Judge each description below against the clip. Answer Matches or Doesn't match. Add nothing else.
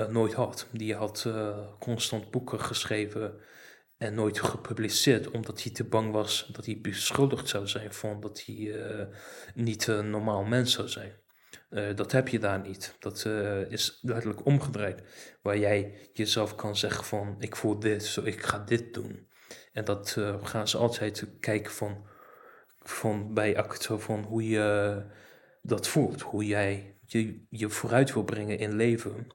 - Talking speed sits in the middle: Matches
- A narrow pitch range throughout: Matches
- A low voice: Matches